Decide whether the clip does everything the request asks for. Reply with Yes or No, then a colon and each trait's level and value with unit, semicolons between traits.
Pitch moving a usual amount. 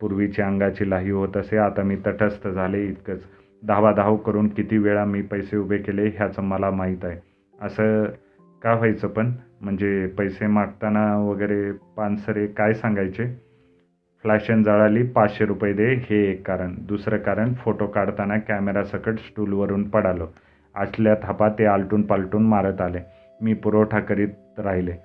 No: narrow, 1.4 semitones